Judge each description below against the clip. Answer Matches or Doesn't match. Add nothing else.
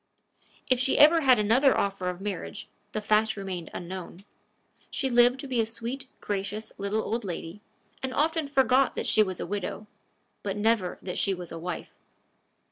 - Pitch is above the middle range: Matches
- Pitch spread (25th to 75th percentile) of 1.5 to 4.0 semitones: Doesn't match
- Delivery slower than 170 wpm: Doesn't match